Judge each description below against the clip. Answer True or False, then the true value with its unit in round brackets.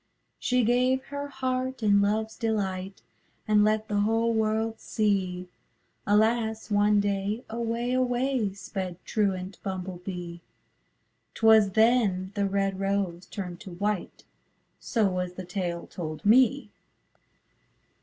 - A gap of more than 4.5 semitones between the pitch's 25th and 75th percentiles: False (3.1 semitones)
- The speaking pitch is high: True (210 Hz)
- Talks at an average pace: False (120 wpm)